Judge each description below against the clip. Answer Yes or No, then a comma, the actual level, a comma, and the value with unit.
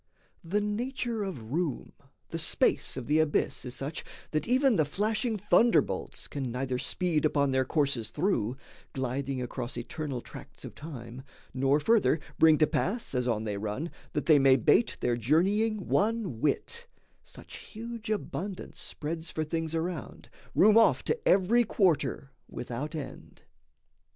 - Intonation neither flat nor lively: No, wide, 7.7 semitones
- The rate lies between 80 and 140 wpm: No, average, 150 wpm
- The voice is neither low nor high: Yes, medium, 155 Hz